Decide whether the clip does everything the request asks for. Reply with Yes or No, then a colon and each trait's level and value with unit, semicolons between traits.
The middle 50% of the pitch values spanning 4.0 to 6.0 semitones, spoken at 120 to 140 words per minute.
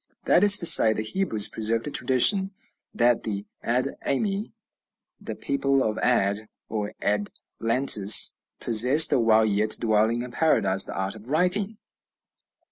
Yes: average, 4.7 semitones; slow, 135 wpm